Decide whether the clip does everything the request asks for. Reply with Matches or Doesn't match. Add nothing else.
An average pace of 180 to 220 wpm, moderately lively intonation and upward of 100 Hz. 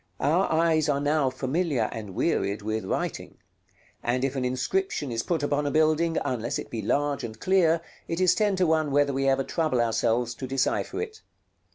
Matches